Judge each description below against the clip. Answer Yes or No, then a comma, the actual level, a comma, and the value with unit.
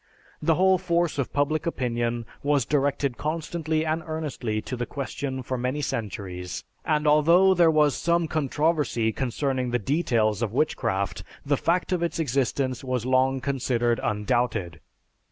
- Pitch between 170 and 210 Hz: No, medium, 140 Hz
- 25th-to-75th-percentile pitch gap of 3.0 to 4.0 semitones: No, average, 4.6 semitones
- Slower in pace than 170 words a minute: Yes, average, 145 wpm